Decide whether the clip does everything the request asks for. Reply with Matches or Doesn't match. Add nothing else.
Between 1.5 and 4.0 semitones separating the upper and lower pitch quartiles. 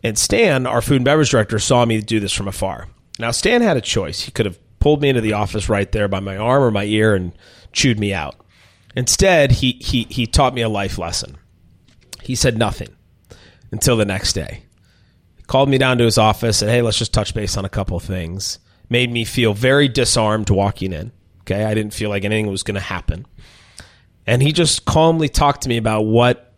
Matches